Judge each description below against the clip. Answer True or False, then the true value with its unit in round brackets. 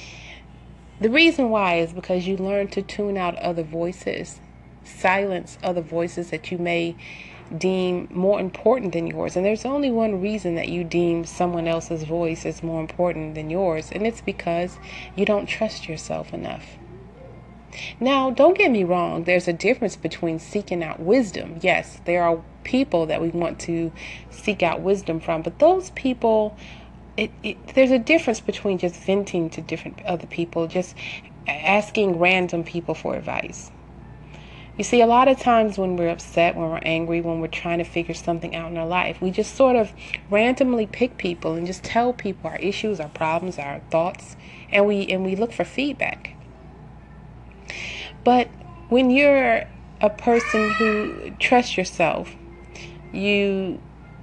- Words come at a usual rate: True (165 wpm)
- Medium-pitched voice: True (180 Hz)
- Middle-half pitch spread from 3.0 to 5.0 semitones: True (4.2 semitones)